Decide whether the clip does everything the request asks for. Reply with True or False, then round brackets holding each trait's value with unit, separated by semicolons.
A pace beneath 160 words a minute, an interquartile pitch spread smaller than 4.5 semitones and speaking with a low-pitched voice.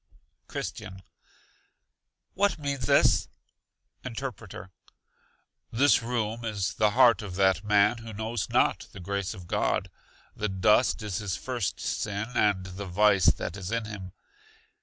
True (135 wpm; 3.3 semitones; 105 Hz)